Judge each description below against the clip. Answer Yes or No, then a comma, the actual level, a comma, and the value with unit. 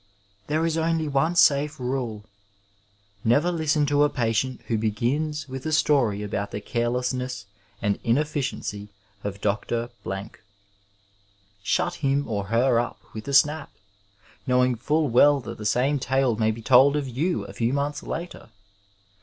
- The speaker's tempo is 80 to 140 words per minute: No, average, 155 wpm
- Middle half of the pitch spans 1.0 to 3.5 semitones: No, average, 4.7 semitones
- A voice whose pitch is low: Yes, low, 130 Hz